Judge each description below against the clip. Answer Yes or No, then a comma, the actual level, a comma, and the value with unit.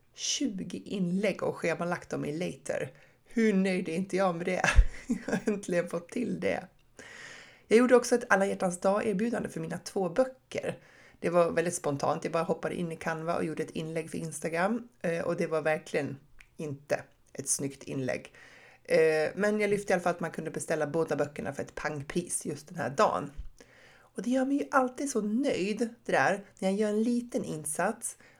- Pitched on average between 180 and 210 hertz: Yes, medium, 185 Hz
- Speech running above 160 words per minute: Yes, average, 190 wpm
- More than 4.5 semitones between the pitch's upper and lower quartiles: Yes, average, 5.0 semitones